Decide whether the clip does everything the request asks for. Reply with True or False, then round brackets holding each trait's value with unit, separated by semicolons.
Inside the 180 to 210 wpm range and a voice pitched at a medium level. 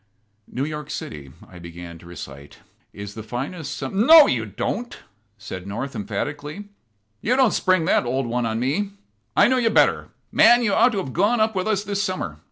True (200 wpm; 145 Hz)